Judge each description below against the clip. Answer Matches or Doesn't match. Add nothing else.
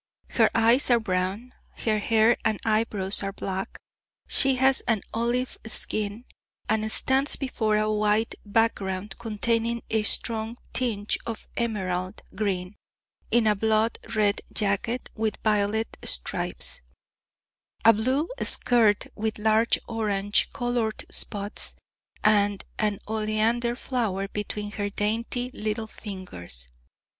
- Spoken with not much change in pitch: Matches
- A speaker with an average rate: Doesn't match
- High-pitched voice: Matches